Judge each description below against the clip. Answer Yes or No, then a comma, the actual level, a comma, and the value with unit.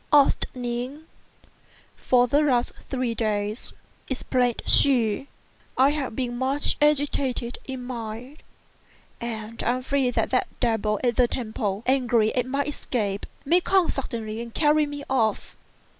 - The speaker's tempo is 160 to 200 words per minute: No, slow, 135 wpm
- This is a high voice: Yes, very high, 250 Hz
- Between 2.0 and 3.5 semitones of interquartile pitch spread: Yes, average, 3.1 semitones